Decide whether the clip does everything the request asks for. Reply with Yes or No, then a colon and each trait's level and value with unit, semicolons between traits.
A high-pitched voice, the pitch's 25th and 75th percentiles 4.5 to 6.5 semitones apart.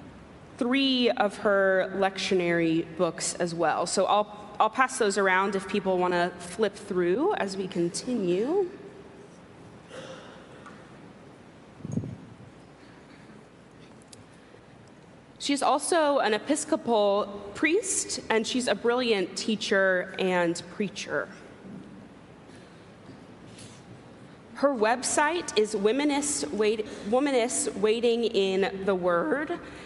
Yes: high, 210 Hz; average, 5.1 semitones